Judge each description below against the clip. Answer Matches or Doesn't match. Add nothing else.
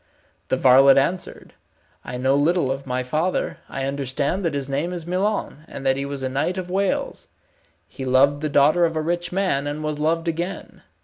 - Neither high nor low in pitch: Matches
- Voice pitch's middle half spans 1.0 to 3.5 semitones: Doesn't match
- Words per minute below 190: Doesn't match